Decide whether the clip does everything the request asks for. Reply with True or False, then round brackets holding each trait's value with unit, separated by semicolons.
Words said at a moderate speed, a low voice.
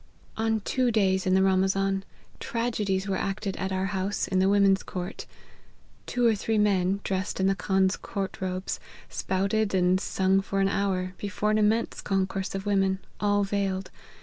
False (175 wpm; 195 Hz)